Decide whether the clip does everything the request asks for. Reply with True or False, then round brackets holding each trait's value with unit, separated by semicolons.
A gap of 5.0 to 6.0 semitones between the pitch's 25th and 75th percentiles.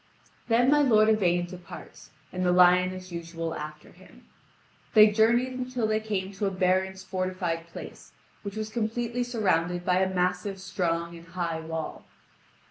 False (3.6 semitones)